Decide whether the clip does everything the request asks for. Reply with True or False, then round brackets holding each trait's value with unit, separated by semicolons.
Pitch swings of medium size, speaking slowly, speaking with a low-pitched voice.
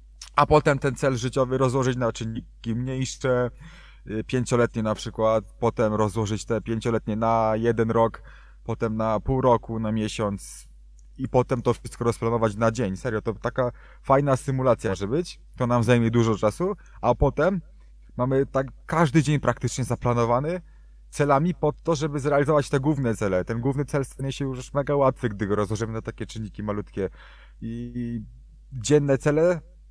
False (3.5 semitones; 155 wpm; 120 Hz)